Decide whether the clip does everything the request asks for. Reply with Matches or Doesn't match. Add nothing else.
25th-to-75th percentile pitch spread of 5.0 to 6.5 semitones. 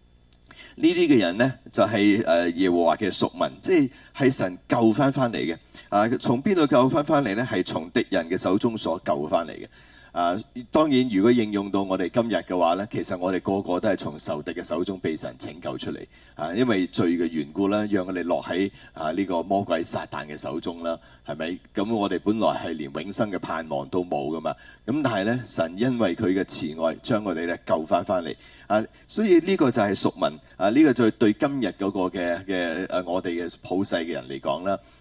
Matches